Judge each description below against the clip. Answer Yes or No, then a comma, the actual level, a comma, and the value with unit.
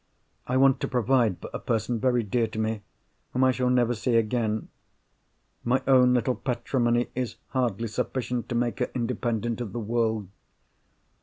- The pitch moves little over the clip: Yes, narrow, 2.0 semitones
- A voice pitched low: Yes, low, 120 Hz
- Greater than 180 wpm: No, average, 155 wpm